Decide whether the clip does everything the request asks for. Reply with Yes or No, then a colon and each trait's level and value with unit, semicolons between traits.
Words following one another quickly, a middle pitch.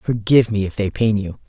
No: fast, 245 wpm; low, 105 Hz